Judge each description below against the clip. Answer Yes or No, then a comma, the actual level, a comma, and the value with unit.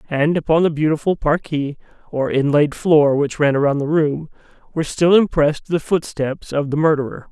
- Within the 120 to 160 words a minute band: No, average, 170 wpm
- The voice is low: No, medium, 150 Hz